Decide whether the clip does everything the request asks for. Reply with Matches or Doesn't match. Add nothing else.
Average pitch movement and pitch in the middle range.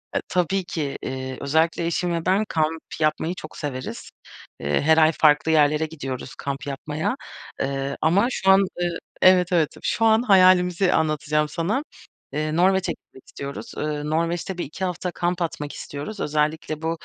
Matches